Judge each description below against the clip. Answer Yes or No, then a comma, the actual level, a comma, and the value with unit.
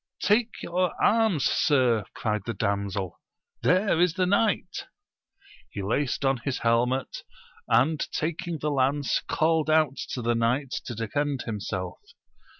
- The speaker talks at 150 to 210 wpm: No, slow, 135 wpm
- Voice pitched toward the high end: No, low, 135 Hz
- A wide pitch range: Yes, wide, 6.0 semitones